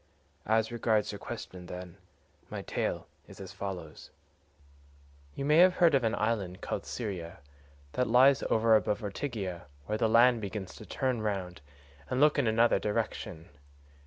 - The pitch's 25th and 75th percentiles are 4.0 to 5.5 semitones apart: Yes, average, 4.4 semitones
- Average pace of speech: Yes, average, 155 wpm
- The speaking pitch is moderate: No, low, 110 Hz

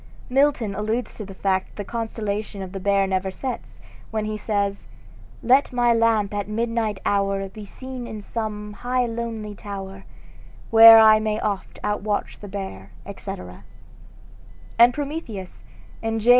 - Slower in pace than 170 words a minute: Yes, average, 150 wpm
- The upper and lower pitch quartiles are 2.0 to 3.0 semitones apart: Yes, narrow, 2.5 semitones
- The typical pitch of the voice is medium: No, high, 215 Hz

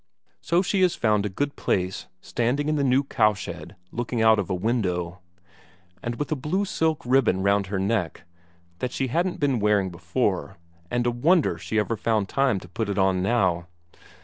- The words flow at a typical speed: Yes, average, 185 wpm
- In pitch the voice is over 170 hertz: No, low, 110 Hz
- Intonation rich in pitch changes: Yes, wide, 6.0 semitones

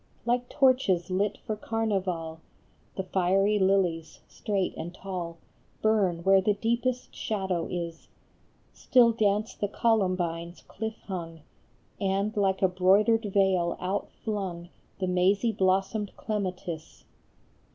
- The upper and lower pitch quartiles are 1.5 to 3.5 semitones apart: Yes, average, 2.9 semitones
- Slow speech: Yes, slow, 110 wpm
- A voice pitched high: Yes, high, 195 Hz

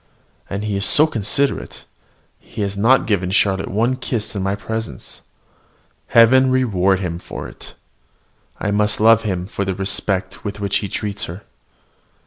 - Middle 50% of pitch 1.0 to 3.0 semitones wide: Yes, narrow, 2.6 semitones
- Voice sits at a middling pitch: No, low, 100 Hz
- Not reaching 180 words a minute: Yes, average, 155 wpm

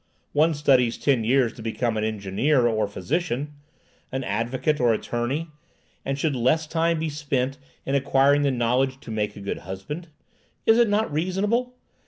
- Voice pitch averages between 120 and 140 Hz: Yes, low, 135 Hz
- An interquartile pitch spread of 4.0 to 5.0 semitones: Yes, average, 4.7 semitones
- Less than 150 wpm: No, average, 165 wpm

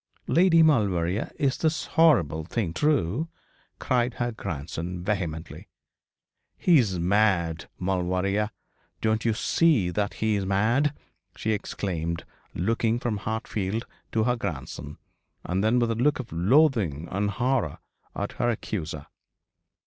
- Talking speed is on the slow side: Yes, slow, 125 wpm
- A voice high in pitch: No, low, 105 Hz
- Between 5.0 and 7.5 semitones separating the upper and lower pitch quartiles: Yes, wide, 5.5 semitones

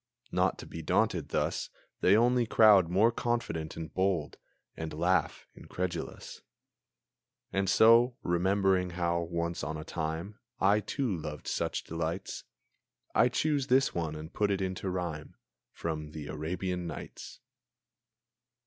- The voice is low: Yes, very low, 90 Hz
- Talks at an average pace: No, slow, 130 wpm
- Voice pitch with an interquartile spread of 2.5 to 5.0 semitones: Yes, average, 4.1 semitones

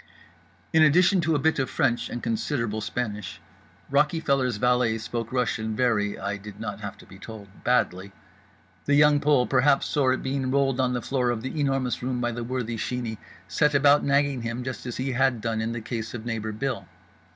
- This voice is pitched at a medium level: No, low, 125 Hz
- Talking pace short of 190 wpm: No, average, 195 wpm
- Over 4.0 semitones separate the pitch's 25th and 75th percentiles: No, average, 3.5 semitones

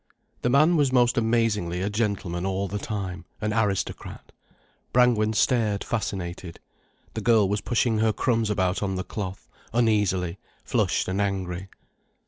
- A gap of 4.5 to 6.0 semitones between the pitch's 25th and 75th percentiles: No, average, 3.2 semitones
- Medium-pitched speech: No, low, 105 Hz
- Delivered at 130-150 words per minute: Yes, average, 140 wpm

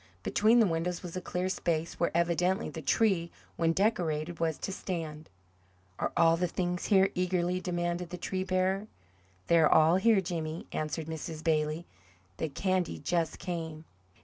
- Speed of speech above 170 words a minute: No, average, 155 wpm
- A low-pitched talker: No, medium, 175 Hz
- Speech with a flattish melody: Yes, narrow, 2.3 semitones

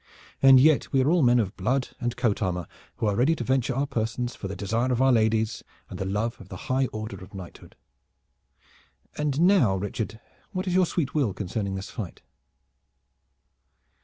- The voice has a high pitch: No, low, 115 Hz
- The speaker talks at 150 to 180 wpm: No, average, 190 wpm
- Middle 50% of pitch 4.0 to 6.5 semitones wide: Yes, average, 4.6 semitones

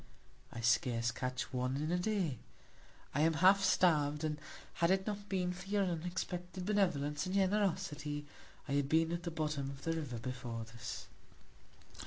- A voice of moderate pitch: Yes, medium, 160 Hz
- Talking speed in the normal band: Yes, average, 165 wpm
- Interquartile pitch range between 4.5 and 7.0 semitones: Yes, average, 4.9 semitones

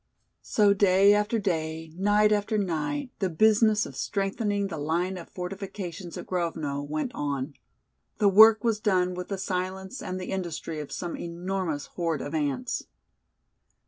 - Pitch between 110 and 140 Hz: No, medium, 185 Hz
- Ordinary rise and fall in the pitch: Yes, average, 3.9 semitones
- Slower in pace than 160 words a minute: Yes, average, 150 wpm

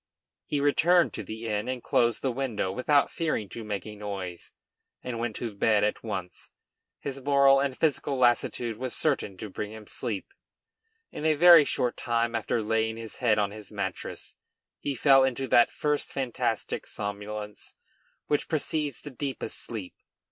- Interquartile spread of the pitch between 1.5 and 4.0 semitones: No, average, 4.6 semitones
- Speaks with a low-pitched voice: Yes, low, 120 Hz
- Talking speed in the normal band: Yes, average, 165 wpm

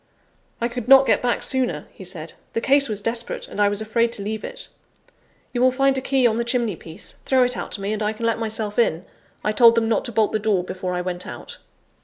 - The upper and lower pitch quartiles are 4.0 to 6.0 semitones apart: No, average, 3.2 semitones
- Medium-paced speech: No, fast, 255 wpm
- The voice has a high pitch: Yes, high, 225 Hz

